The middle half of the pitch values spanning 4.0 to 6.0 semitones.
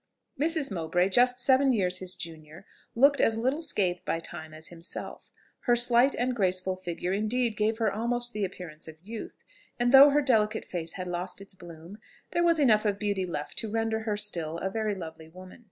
Yes: average, 5.3 semitones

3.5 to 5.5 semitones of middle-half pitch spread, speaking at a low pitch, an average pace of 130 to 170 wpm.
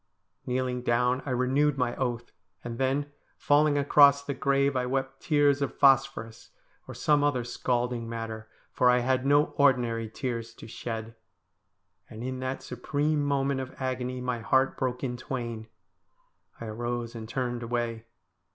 No: narrow, 2.4 semitones; low, 125 Hz; average, 150 wpm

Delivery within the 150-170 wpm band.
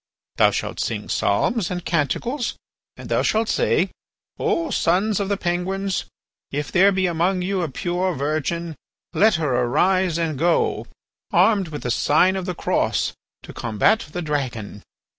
Yes: average, 155 wpm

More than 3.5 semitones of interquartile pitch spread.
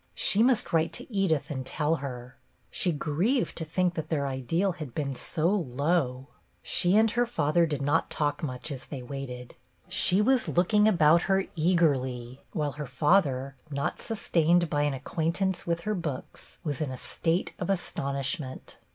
Yes: average, 4.6 semitones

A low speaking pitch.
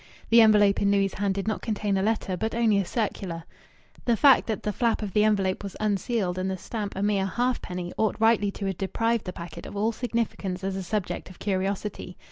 No: high, 200 Hz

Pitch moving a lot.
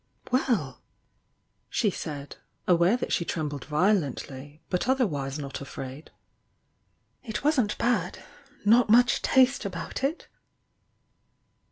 Yes: wide, 8.9 semitones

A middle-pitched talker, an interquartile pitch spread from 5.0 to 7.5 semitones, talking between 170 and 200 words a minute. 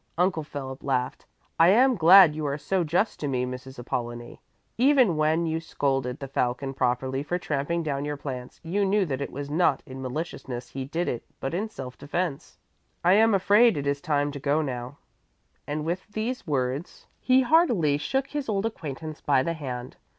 Yes: medium, 150 Hz; average, 5.3 semitones; average, 185 wpm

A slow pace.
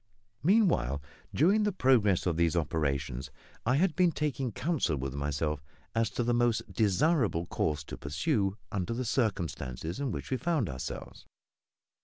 No: average, 150 wpm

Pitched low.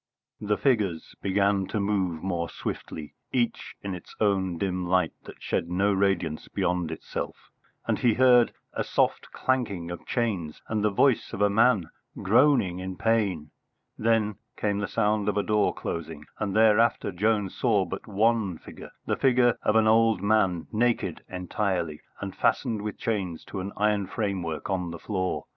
Yes: low, 100 Hz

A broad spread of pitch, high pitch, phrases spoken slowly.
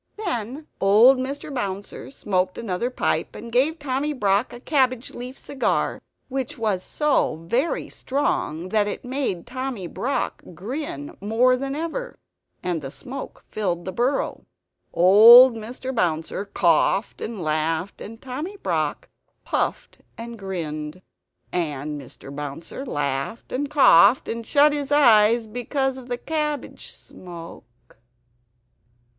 Yes: wide, 6.7 semitones; high, 230 Hz; slow, 125 wpm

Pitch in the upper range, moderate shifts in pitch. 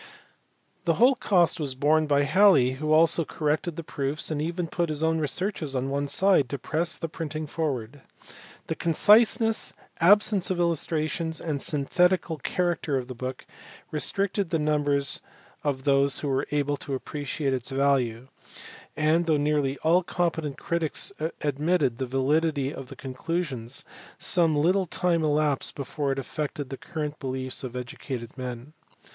No: medium, 150 Hz; average, 3.6 semitones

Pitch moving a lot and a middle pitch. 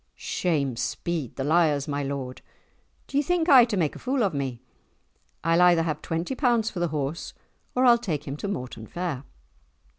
Yes: wide, 7.4 semitones; medium, 165 Hz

